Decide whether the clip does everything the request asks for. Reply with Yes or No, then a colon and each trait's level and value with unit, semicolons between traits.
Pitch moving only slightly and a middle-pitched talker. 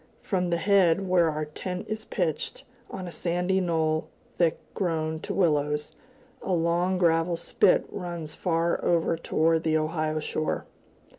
Yes: narrow, 2.3 semitones; medium, 170 Hz